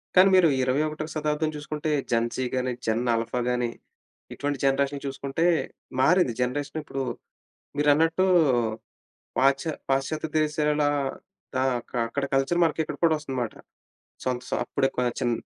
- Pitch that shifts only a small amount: No, average, 3.2 semitones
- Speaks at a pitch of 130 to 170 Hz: Yes, medium, 140 Hz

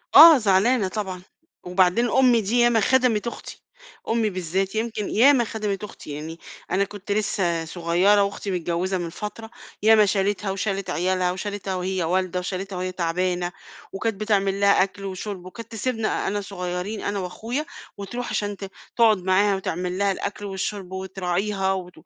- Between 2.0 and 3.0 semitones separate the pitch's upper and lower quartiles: Yes, narrow, 2.6 semitones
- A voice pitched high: Yes, high, 195 Hz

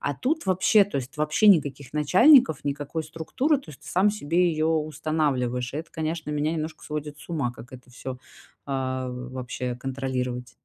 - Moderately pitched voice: Yes, medium, 150 Hz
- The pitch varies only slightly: No, average, 4.0 semitones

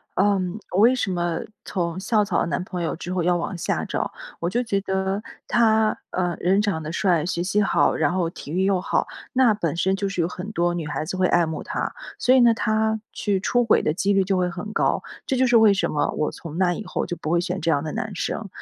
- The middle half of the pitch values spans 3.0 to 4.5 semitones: Yes, average, 3.4 semitones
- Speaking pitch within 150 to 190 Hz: Yes, medium, 185 Hz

